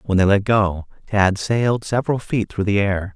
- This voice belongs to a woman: No, male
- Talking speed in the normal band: No, fast, 210 wpm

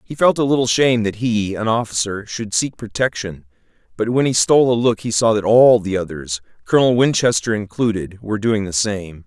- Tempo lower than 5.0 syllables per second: No, 5.4 syllables/s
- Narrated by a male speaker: Yes, male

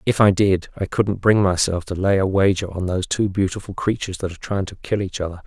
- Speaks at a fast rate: Yes, fast, 250 wpm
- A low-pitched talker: Yes, very low, 95 Hz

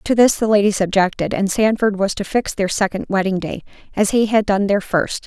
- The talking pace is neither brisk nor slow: No, fast, 230 wpm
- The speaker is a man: No, female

